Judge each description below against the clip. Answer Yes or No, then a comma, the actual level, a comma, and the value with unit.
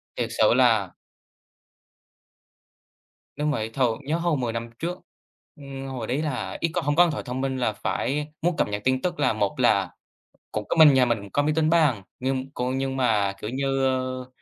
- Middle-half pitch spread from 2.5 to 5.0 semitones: Yes, average, 3.4 semitones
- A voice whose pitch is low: Yes, low, 130 Hz